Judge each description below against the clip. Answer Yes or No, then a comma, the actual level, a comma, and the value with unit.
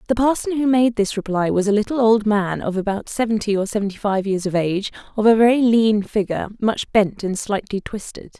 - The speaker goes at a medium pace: No, fast, 215 wpm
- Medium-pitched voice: No, high, 210 Hz